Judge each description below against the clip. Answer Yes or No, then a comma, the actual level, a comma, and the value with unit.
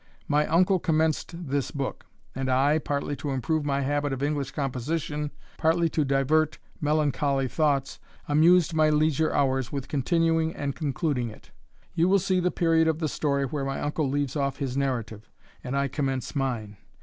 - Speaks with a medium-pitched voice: Yes, medium, 145 Hz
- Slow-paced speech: No, average, 170 wpm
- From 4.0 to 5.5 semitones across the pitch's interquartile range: No, narrow, 2.6 semitones